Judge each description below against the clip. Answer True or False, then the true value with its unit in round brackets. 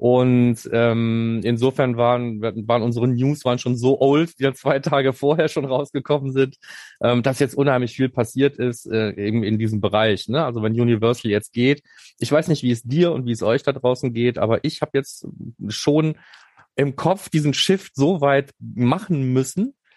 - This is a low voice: True (130 Hz)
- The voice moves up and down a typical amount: True (3.2 semitones)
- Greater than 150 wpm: True (190 wpm)